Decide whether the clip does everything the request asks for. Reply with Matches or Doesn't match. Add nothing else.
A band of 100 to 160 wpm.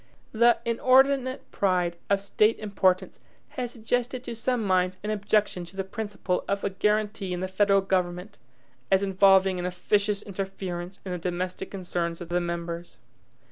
Matches